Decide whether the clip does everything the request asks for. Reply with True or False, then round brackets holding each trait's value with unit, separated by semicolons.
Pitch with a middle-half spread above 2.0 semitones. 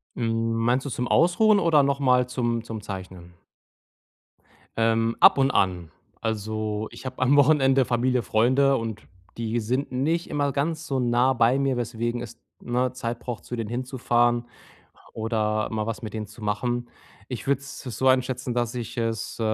True (2.5 semitones)